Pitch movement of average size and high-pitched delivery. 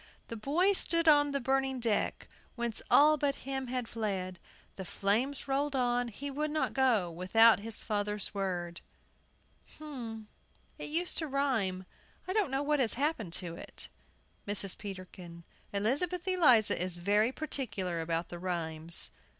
No: wide, 6.8 semitones; high, 230 Hz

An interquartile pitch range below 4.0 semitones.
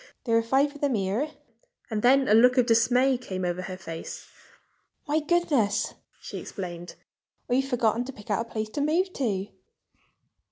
No: average, 4.8 semitones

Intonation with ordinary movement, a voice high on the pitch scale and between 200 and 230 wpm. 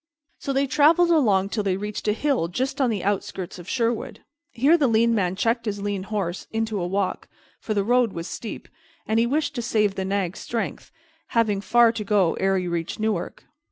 Yes: average, 3.7 semitones; high, 215 Hz; fast, 205 wpm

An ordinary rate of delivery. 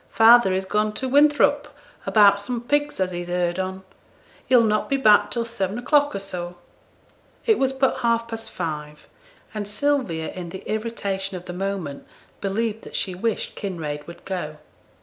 Yes: average, 170 wpm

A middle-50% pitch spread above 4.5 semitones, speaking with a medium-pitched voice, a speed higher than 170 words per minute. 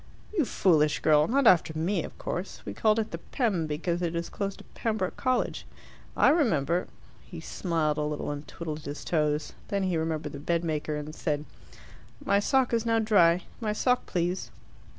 Yes: wide, 5.6 semitones; medium, 170 Hz; average, 185 wpm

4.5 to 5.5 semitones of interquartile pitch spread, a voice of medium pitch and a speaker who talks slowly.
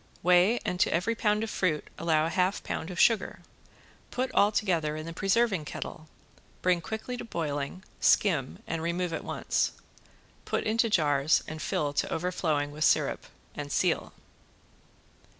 No: average, 4.8 semitones; medium, 175 Hz; average, 155 wpm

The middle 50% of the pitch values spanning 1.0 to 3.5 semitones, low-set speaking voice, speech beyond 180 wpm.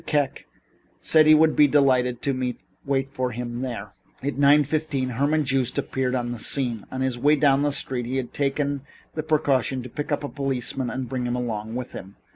Yes: narrow, 2.6 semitones; low, 130 Hz; fast, 205 wpm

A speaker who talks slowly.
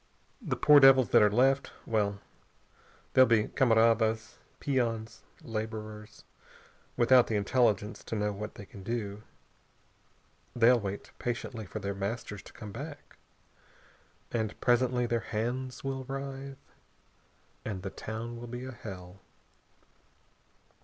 Yes: slow, 125 wpm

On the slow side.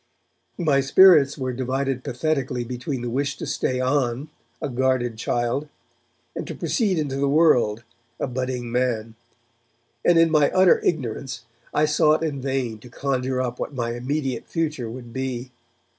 No: average, 155 wpm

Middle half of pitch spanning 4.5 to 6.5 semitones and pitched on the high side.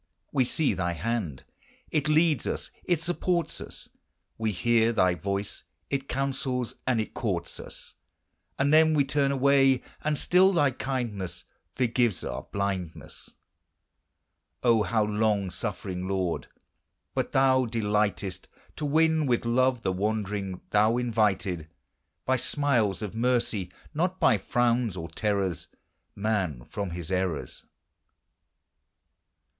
No: wide, 5.6 semitones; low, 115 Hz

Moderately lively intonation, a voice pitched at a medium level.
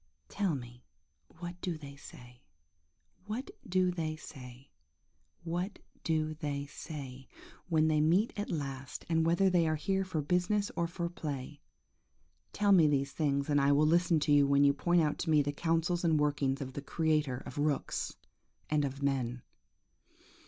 Yes: average, 3.6 semitones; medium, 155 Hz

